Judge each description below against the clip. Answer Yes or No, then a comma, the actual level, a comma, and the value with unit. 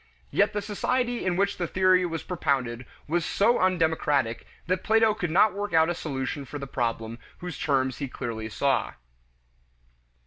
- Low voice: No, medium, 165 Hz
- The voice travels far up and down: Yes, wide, 6.1 semitones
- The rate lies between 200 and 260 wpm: No, average, 165 wpm